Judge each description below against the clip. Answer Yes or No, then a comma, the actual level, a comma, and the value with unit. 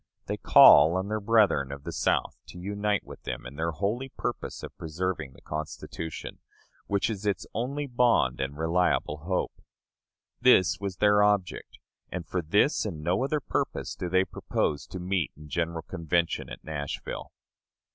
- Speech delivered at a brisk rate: No, average, 165 wpm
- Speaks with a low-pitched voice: Yes, very low, 90 Hz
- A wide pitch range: No, average, 4.4 semitones